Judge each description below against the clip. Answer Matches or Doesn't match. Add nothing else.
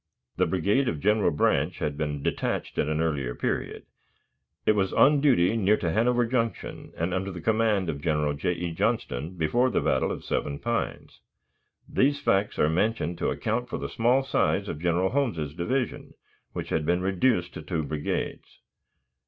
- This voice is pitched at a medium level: Doesn't match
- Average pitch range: Doesn't match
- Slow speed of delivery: Doesn't match